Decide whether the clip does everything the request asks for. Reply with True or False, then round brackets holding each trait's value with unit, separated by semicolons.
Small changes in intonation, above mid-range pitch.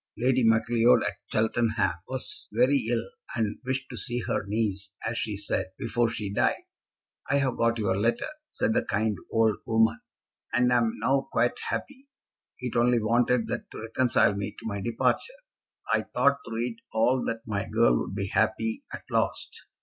False (2.2 semitones; 115 Hz)